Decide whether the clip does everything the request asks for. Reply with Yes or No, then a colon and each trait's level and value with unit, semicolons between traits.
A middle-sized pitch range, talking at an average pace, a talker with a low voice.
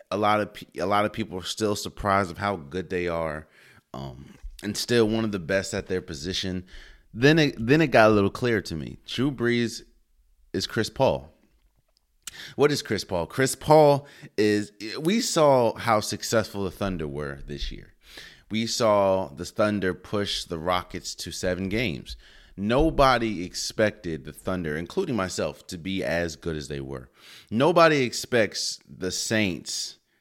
Yes: average, 4.3 semitones; average, 165 wpm; low, 100 Hz